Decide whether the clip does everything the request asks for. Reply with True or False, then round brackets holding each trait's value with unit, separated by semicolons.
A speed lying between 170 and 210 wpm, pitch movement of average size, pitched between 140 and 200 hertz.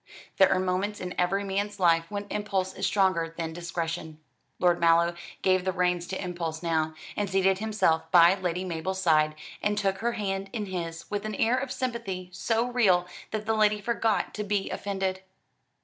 True (180 wpm; 3.1 semitones; 190 Hz)